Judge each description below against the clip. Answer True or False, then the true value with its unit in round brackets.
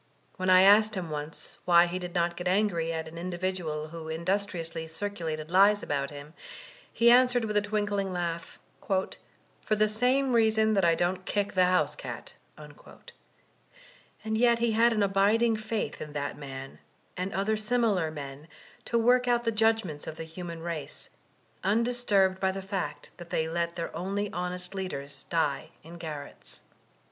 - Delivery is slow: False (165 wpm)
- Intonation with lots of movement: False (4.5 semitones)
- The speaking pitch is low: False (185 Hz)